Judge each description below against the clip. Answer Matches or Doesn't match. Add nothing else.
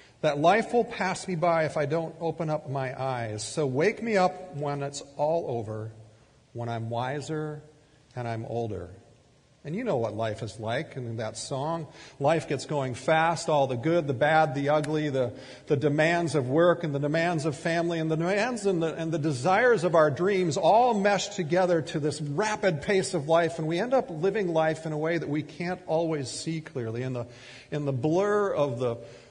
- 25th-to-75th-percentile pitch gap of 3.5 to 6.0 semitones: Matches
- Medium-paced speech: Doesn't match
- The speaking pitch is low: Doesn't match